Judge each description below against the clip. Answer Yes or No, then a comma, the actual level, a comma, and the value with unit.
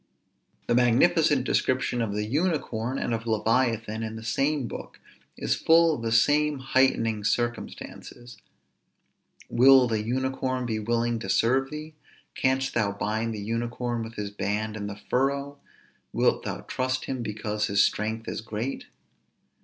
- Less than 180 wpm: Yes, average, 150 wpm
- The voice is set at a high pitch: No, low, 120 Hz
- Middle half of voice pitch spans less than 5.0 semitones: Yes, average, 3.2 semitones